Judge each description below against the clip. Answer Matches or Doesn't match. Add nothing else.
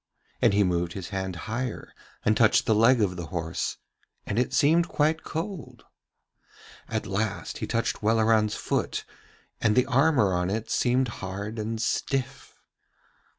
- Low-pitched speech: Matches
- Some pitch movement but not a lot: Matches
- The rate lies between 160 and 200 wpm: Doesn't match